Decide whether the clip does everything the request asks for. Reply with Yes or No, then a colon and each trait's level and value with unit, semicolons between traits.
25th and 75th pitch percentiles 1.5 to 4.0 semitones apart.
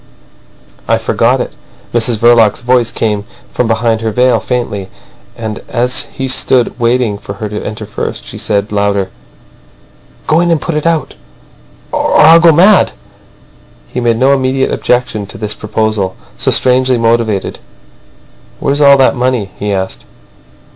Yes: average, 3.5 semitones